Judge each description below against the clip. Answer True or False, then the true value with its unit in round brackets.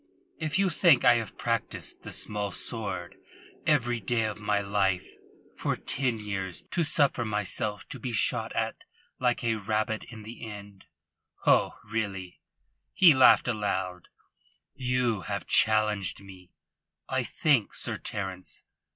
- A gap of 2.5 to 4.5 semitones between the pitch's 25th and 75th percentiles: True (3.6 semitones)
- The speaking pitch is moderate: False (110 Hz)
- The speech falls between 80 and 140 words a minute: True (135 wpm)